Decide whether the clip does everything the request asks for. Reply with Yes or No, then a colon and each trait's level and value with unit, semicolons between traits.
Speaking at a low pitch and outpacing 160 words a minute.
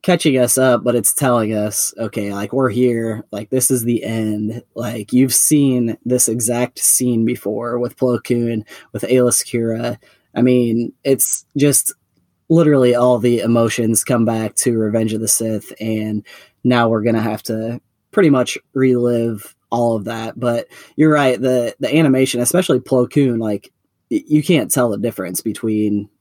Yes: low, 120 Hz; average, 170 wpm